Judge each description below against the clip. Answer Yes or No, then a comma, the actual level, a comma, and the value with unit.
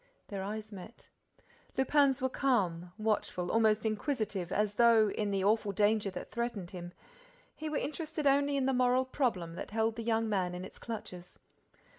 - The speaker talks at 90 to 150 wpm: No, average, 170 wpm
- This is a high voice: Yes, high, 220 Hz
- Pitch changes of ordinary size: Yes, average, 4.5 semitones